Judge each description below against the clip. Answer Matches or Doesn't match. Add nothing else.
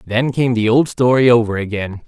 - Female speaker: Doesn't match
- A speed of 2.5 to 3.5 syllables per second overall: Doesn't match